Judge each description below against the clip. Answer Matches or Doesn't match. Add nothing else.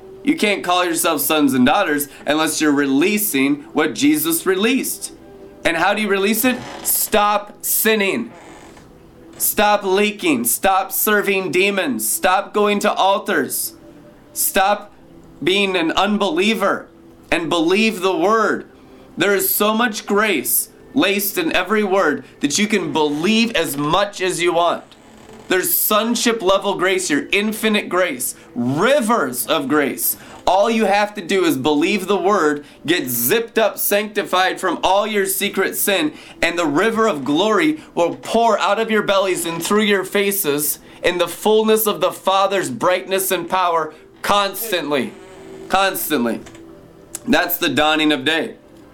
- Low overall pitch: Doesn't match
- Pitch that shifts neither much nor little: Matches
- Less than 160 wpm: Matches